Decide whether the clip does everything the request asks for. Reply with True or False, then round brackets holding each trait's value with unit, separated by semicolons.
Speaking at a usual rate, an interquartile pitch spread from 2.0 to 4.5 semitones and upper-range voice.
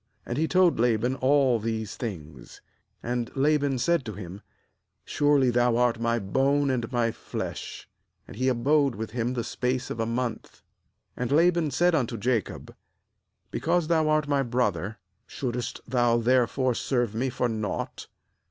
False (160 wpm; 3.3 semitones; 125 Hz)